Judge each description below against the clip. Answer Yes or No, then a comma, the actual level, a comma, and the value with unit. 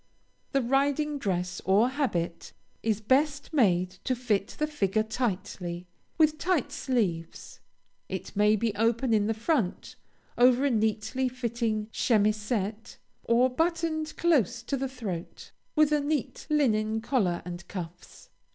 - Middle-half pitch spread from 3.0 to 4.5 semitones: No, average, 5.1 semitones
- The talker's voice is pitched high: Yes, high, 235 Hz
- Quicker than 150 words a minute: No, slow, 135 wpm